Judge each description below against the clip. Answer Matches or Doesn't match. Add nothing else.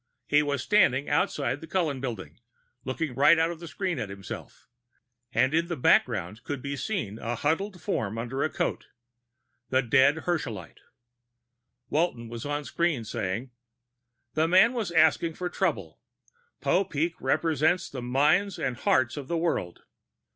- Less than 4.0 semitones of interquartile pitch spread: Doesn't match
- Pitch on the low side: Doesn't match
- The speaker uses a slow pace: Doesn't match